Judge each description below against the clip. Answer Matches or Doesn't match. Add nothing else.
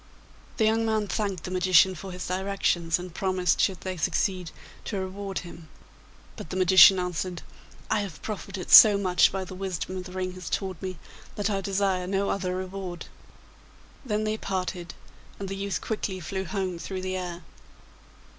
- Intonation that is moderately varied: Doesn't match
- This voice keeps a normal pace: Matches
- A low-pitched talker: Doesn't match